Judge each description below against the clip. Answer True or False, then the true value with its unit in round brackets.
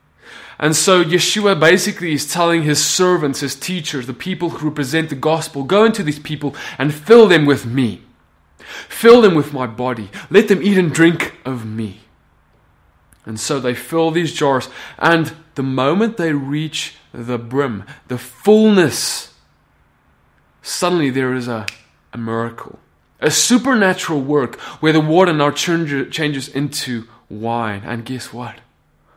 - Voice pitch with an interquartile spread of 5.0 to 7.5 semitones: True (5.3 semitones)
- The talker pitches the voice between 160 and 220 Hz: False (145 Hz)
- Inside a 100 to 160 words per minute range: True (145 wpm)